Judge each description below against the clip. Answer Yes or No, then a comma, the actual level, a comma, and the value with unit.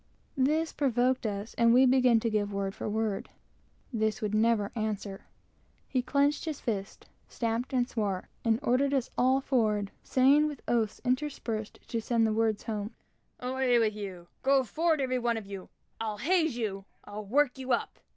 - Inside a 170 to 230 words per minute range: Yes, average, 175 wpm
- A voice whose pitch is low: No, high, 230 Hz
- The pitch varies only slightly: No, average, 3.6 semitones